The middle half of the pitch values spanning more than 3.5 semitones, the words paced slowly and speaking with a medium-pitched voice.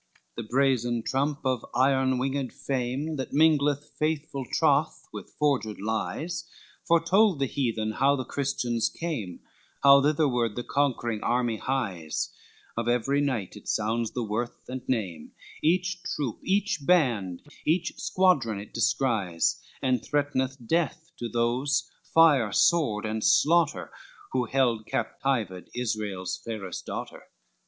No: average, 4.3 semitones; slow, 130 wpm; low, 130 Hz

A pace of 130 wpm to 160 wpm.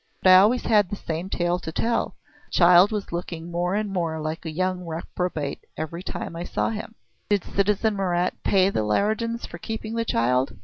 No: average, 195 wpm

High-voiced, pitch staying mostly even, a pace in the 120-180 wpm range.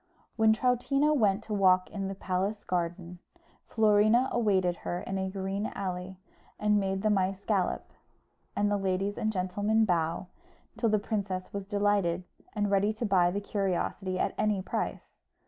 Yes: high, 200 Hz; narrow, 2.2 semitones; average, 160 wpm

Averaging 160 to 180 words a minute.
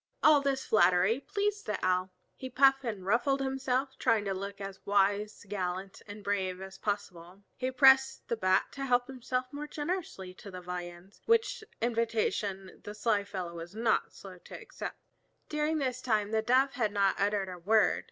Yes: average, 175 wpm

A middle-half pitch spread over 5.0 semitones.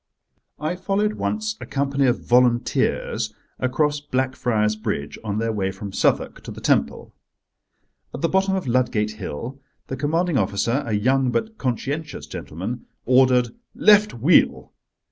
Yes: wide, 5.4 semitones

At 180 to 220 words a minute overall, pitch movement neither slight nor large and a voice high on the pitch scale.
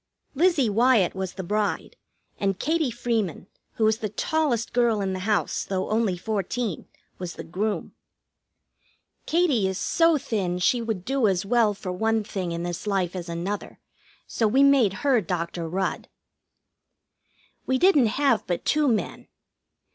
No: average, 155 wpm; average, 4.7 semitones; high, 215 Hz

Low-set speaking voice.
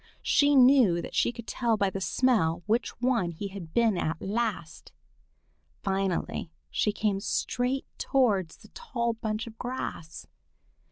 No: high, 215 Hz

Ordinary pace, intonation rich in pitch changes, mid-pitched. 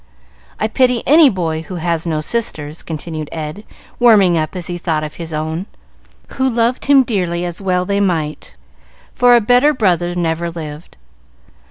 Yes: average, 165 wpm; wide, 5.7 semitones; medium, 175 Hz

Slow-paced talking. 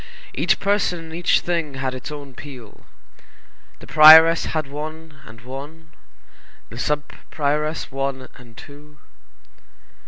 Yes: slow, 125 wpm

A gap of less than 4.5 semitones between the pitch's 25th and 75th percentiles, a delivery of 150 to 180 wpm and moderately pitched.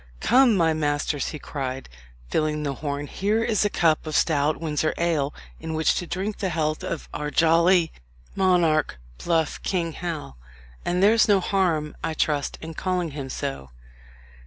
Yes: average, 3.2 semitones; average, 160 wpm; medium, 160 Hz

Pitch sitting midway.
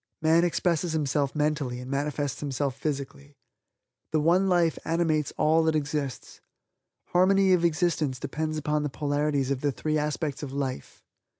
Yes: medium, 150 Hz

